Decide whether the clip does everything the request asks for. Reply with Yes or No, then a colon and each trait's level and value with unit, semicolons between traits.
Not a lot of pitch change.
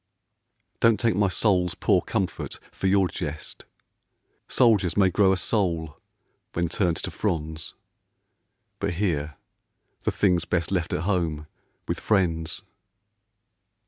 No: average, 3.5 semitones